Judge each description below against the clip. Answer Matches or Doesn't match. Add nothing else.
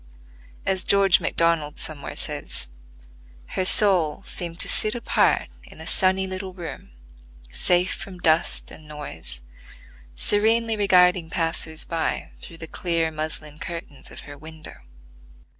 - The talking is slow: Matches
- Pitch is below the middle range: Doesn't match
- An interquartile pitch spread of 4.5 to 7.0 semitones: Doesn't match